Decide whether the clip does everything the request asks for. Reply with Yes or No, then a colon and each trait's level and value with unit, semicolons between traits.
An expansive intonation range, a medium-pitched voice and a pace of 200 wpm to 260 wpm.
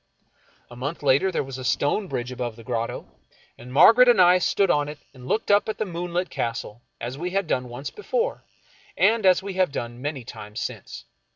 Yes: wide, 7.3 semitones; medium, 145 Hz; fast, 205 wpm